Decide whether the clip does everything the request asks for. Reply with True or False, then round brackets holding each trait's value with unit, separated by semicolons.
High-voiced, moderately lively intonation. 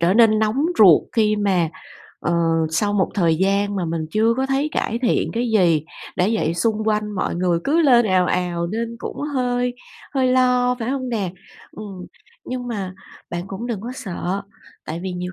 True (210 Hz; 4.9 semitones)